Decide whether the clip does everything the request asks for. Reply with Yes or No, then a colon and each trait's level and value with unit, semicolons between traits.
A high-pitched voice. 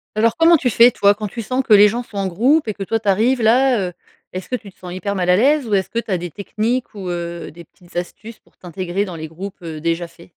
Yes: high, 200 Hz